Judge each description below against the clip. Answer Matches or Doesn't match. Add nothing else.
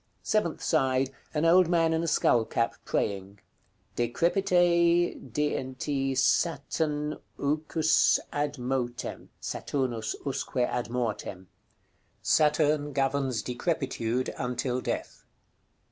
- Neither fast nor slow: Doesn't match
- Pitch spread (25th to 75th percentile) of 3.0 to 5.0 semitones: Matches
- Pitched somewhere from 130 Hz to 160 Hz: Matches